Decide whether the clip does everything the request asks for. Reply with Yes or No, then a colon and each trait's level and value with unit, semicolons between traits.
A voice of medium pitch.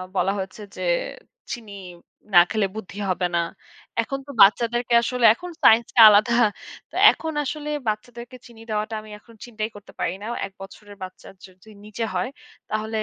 No: high, 220 Hz